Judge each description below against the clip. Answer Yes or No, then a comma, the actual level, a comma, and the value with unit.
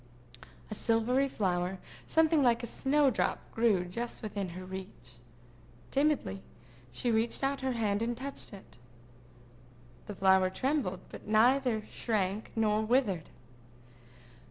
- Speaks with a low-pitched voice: No, high, 220 Hz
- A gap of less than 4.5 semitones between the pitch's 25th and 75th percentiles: No, average, 5.1 semitones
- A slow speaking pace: Yes, slow, 125 wpm